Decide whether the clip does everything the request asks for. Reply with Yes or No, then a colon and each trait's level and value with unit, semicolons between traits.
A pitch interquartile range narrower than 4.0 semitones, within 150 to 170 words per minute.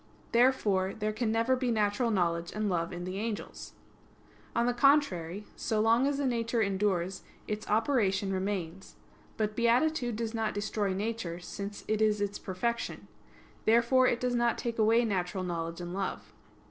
Yes: average, 3.6 semitones; average, 160 wpm